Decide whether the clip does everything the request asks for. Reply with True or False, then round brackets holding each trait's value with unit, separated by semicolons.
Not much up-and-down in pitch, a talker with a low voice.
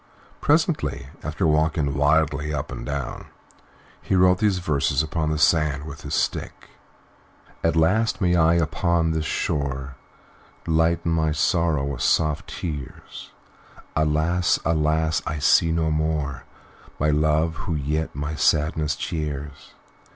True (1.9 semitones; 80 Hz)